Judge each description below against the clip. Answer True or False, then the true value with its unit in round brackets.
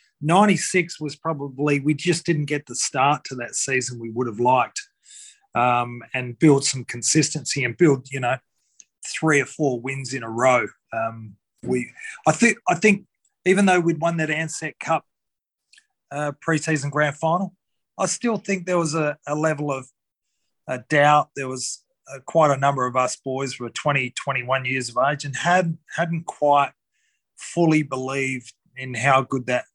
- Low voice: False (145 Hz)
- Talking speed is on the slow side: False (175 wpm)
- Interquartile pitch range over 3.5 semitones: True (4.4 semitones)